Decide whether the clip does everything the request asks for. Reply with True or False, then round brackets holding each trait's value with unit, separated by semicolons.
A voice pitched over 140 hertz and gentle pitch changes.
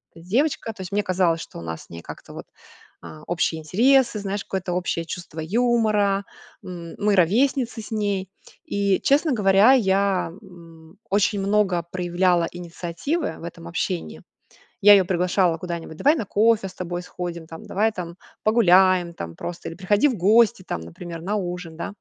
False (185 Hz; 3.5 semitones)